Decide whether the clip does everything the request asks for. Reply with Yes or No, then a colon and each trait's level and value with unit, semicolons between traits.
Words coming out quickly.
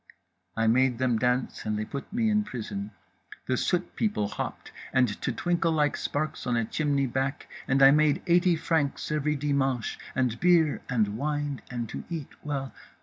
No: average, 175 wpm